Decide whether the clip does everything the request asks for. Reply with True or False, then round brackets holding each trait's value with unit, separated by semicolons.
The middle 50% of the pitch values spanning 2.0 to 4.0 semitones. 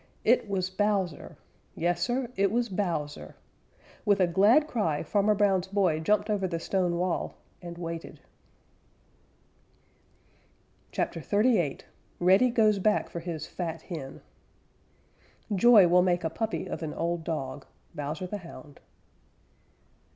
True (3.7 semitones)